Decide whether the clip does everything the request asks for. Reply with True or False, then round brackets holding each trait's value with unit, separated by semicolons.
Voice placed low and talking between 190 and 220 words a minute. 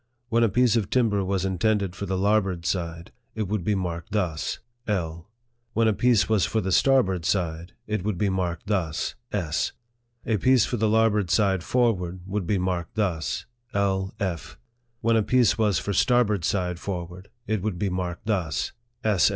True (100 Hz; 195 wpm)